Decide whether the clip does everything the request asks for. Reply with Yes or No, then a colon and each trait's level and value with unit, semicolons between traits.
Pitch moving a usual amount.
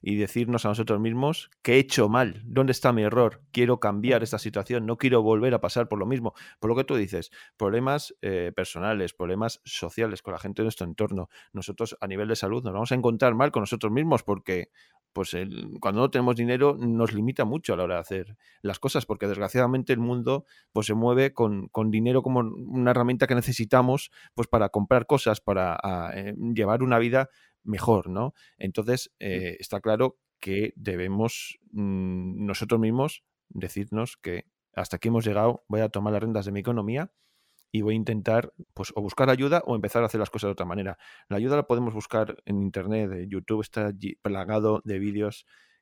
Yes: average, 3.4 semitones